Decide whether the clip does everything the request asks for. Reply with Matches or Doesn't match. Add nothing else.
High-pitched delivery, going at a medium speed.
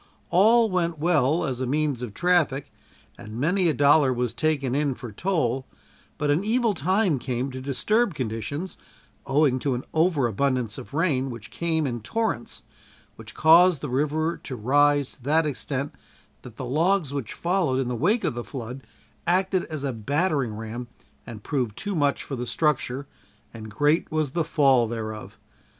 Doesn't match